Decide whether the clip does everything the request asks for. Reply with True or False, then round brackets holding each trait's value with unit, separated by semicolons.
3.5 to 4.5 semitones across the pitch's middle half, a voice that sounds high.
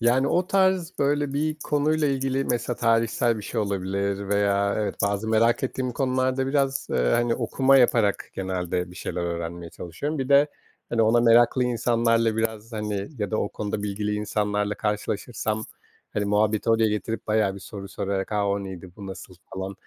False (4.0 semitones; 110 Hz)